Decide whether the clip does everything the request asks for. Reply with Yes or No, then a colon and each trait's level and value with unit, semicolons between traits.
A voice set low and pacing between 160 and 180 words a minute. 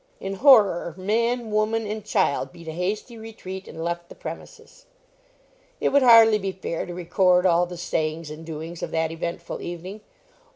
No: medium, 185 Hz; average, 170 wpm